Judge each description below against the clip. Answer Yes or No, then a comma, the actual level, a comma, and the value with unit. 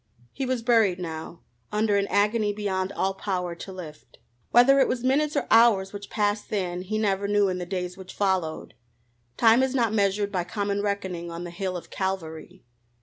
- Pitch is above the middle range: Yes, high, 200 Hz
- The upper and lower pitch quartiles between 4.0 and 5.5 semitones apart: No, average, 3.0 semitones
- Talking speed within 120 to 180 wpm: No, average, 190 wpm